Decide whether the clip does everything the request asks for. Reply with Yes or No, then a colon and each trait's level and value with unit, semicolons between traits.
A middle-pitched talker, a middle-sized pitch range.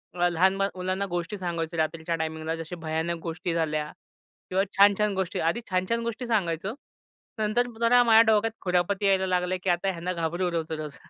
Yes: medium, 180 Hz; average, 3.2 semitones